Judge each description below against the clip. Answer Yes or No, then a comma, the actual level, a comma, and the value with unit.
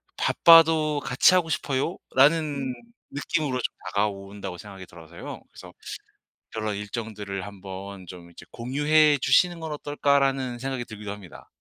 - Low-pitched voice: Yes, low, 125 Hz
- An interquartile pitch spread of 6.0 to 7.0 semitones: Yes, wide, 6.6 semitones